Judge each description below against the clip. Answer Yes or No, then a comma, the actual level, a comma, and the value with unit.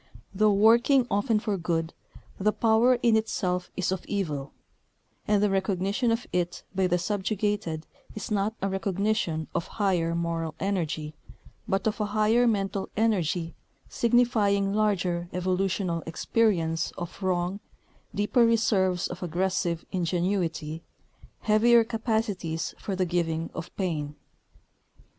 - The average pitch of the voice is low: No, high, 195 Hz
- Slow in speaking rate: Yes, slow, 125 wpm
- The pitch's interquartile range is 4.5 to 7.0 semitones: No, average, 3.8 semitones